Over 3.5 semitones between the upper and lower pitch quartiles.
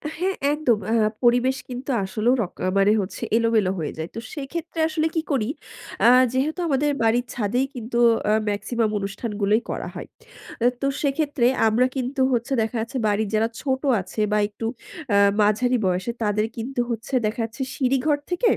Yes: average, 4.0 semitones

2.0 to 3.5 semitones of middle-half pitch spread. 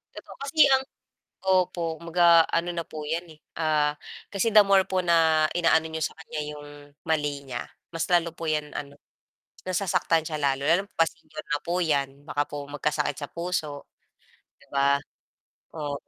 Yes: average, 2.8 semitones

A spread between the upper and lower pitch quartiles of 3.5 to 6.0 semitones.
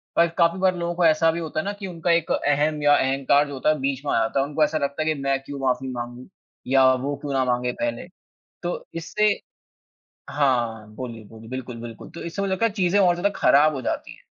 Yes: average, 4.3 semitones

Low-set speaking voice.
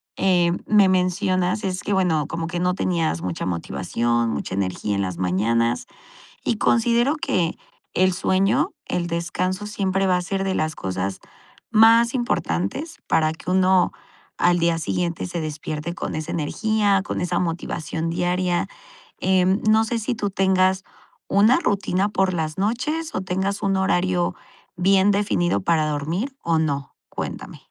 No: medium, 180 Hz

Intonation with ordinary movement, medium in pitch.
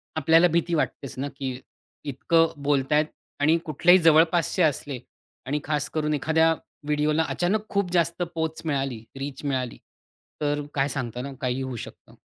Yes: average, 3.1 semitones; medium, 150 Hz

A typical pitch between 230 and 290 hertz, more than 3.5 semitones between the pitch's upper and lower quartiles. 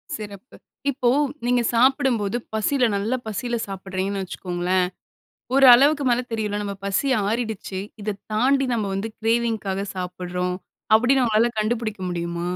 No: high, 215 Hz; average, 3.9 semitones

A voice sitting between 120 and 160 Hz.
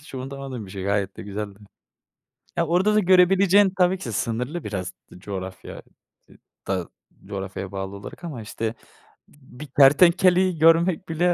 Yes: low, 135 Hz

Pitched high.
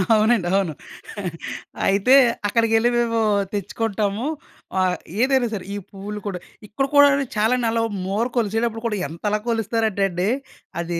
Yes: high, 215 Hz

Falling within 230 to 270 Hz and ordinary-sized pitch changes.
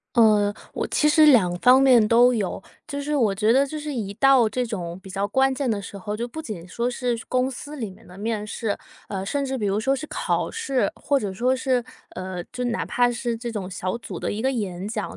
Yes: high, 235 Hz; average, 4.5 semitones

